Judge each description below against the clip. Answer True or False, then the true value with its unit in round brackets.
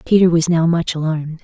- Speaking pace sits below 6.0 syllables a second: False (6.1 syllables/s)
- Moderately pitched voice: True (165 Hz)